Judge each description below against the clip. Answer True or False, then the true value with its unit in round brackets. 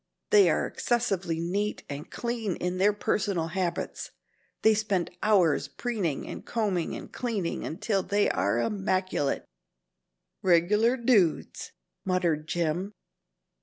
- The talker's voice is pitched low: False (190 Hz)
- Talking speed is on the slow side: True (120 wpm)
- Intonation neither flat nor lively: True (4.0 semitones)